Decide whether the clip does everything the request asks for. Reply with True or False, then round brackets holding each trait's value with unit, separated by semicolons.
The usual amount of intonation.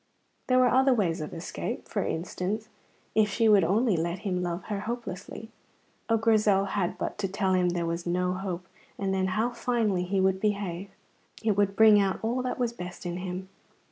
True (3.3 semitones)